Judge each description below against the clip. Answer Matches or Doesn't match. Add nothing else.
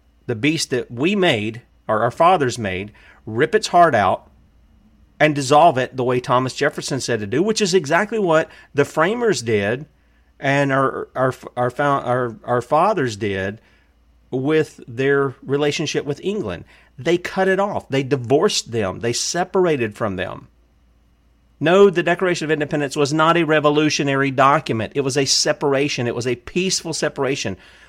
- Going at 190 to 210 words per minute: Doesn't match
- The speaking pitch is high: Doesn't match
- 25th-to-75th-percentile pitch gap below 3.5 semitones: Doesn't match